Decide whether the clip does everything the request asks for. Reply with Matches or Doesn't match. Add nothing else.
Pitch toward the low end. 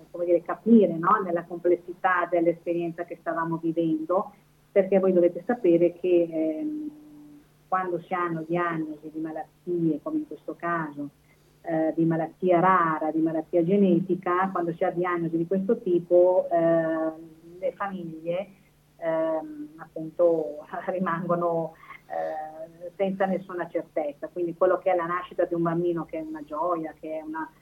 Doesn't match